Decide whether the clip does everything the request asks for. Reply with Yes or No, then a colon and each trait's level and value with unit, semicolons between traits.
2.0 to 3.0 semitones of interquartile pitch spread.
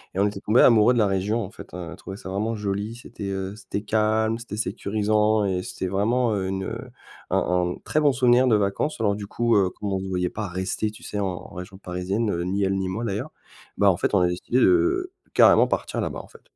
Yes: narrow, 2.6 semitones